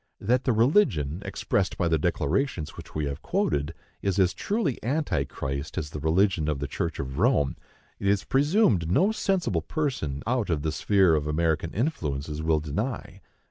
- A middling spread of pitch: No, wide, 8.4 semitones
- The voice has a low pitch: Yes, very low, 85 Hz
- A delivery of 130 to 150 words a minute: No, average, 170 wpm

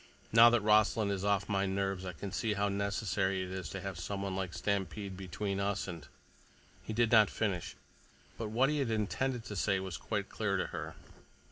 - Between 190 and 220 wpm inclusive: Yes, average, 200 wpm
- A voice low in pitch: Yes, low, 100 Hz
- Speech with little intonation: Yes, narrow, 2.2 semitones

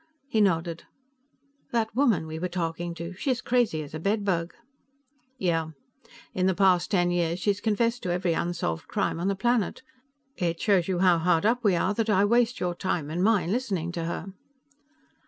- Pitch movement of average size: Yes, average, 3.8 semitones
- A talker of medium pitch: Yes, medium, 180 Hz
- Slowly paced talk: No, average, 180 wpm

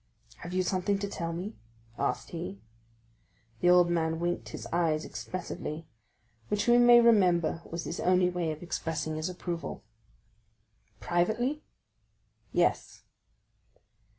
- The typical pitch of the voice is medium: Yes, medium, 175 Hz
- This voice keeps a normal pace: No, slow, 125 wpm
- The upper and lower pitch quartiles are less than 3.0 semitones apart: Yes, narrow, 2.4 semitones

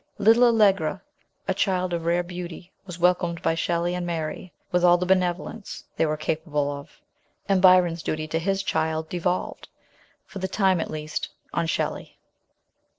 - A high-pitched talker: No, medium, 175 Hz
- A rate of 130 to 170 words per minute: Yes, average, 160 wpm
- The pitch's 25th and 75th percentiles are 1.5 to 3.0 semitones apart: Yes, narrow, 2.4 semitones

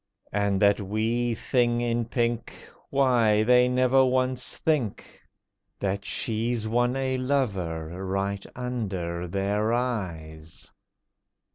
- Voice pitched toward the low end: Yes, low, 115 Hz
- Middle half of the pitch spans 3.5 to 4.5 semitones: Yes, average, 4.1 semitones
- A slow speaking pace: Yes, slow, 105 wpm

